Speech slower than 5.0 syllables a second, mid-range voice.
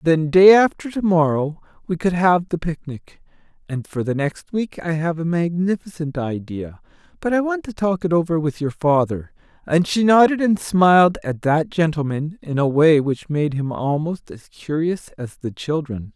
Yes: 4.6 syllables/s; medium, 165 Hz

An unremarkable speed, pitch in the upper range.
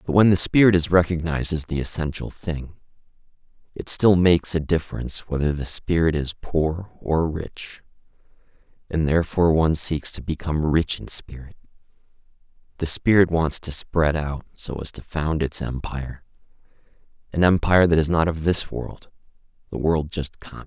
No: average, 155 wpm; very low, 80 Hz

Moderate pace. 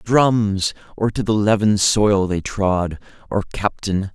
Yes: average, 145 wpm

